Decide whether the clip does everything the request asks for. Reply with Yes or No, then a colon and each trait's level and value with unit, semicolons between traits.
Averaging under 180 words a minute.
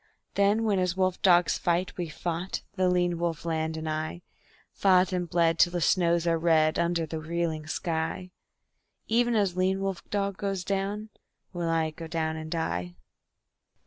Yes: average, 170 wpm